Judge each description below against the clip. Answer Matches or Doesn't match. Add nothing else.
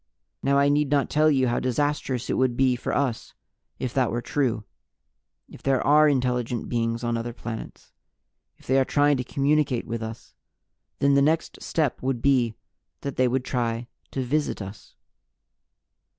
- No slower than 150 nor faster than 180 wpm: Matches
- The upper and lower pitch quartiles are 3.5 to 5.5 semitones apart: Doesn't match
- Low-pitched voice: Matches